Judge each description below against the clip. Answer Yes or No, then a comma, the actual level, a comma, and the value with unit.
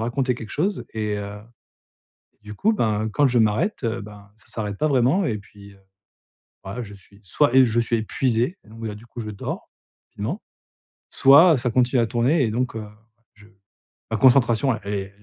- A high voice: No, low, 115 Hz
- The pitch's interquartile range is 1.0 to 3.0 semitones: No, average, 3.8 semitones